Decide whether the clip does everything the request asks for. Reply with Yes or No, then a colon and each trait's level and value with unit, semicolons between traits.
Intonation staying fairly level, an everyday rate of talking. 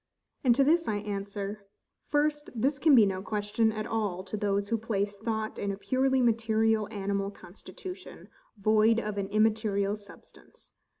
Yes: narrow, 2.2 semitones; average, 160 wpm